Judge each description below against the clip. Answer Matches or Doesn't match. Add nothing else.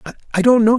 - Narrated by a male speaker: Matches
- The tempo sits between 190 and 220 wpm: Doesn't match